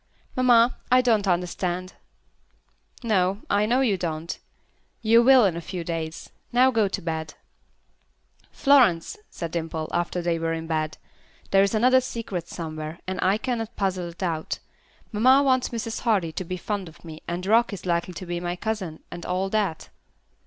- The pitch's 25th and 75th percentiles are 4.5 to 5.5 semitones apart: Yes, average, 5.0 semitones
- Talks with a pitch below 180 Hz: No, medium, 185 Hz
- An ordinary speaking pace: Yes, average, 170 wpm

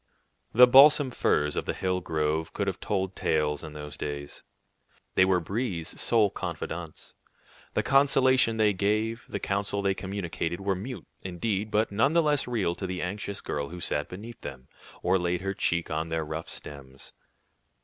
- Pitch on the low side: Yes, very low, 95 Hz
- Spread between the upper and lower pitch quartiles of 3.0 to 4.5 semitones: No, average, 5.0 semitones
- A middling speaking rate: Yes, average, 170 wpm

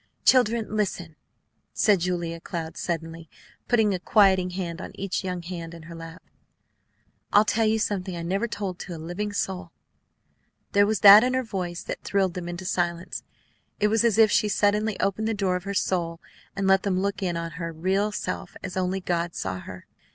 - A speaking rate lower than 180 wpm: No, average, 195 wpm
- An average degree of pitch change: Yes, average, 3.2 semitones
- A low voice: No, medium, 185 Hz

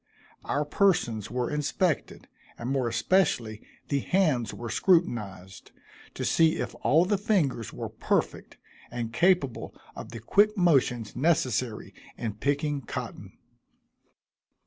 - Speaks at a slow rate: Yes, slow, 120 wpm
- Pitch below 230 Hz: Yes, medium, 140 Hz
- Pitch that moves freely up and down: Yes, wide, 6.5 semitones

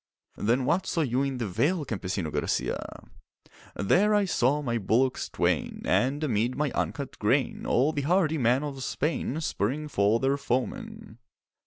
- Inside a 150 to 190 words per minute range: Yes, average, 155 wpm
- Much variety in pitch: No, average, 4.4 semitones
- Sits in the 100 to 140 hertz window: Yes, low, 135 Hz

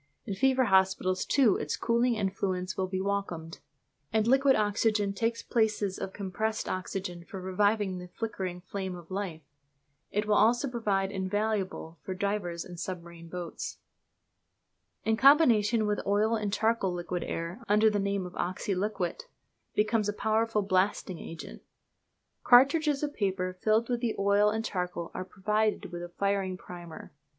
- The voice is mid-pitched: No, high, 200 Hz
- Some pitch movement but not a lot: Yes, average, 3.0 semitones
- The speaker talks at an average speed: Yes, average, 150 wpm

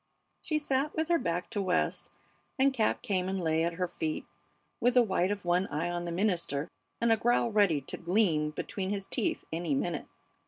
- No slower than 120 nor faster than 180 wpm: No, average, 200 wpm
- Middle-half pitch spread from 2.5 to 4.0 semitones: No, average, 4.9 semitones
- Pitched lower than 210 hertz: Yes, medium, 185 Hz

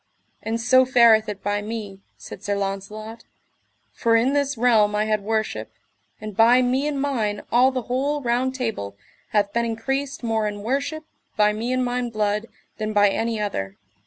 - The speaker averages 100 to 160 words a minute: No, average, 175 wpm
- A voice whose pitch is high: Yes, high, 225 Hz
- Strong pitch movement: No, average, 3.2 semitones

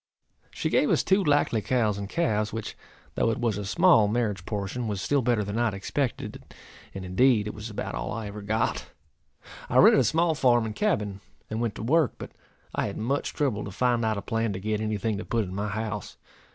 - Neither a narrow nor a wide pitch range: Yes, average, 3.1 semitones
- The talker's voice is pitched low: Yes, low, 110 Hz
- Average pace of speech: No, fast, 225 wpm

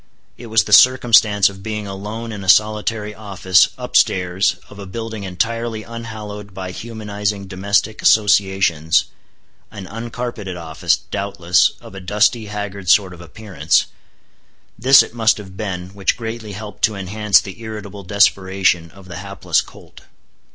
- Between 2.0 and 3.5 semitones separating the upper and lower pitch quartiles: Yes, narrow, 2.4 semitones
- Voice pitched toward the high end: No, low, 100 Hz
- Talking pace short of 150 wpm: Yes, average, 140 wpm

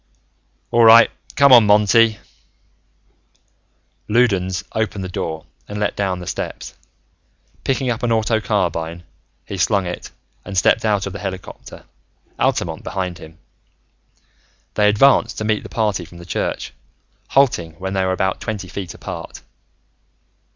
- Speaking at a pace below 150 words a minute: Yes, average, 140 wpm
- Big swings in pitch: No, average, 3.3 semitones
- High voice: No, low, 100 Hz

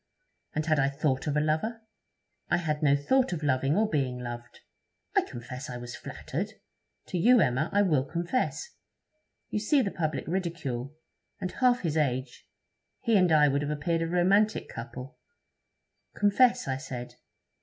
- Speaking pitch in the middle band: Yes, medium, 155 Hz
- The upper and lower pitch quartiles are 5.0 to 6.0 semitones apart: Yes, wide, 5.5 semitones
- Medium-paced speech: Yes, average, 165 wpm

